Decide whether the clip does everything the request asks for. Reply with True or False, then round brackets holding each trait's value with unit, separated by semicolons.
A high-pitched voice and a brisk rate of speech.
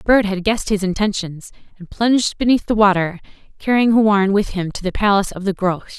True (200 Hz; 220 wpm)